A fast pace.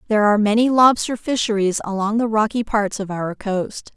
No: average, 180 wpm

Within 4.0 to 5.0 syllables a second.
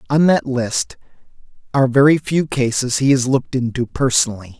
No: 5.5 syllables/s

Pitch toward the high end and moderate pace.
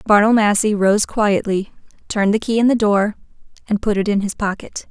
Yes: high, 210 Hz; average, 195 wpm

